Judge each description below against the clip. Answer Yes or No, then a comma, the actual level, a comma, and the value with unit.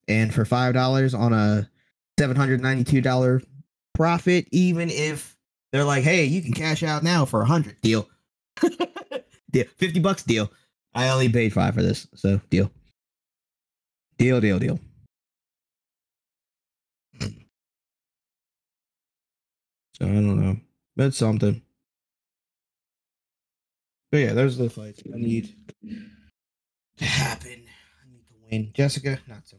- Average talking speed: No, slow, 130 wpm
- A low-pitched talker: Yes, low, 125 Hz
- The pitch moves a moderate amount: No, wide, 5.7 semitones